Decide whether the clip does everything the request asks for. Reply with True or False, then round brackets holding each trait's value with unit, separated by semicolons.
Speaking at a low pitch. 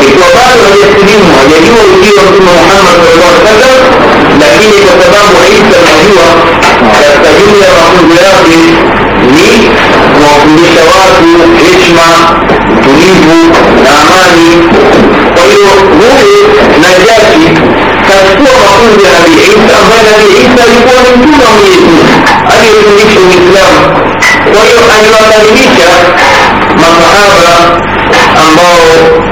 False (190 Hz)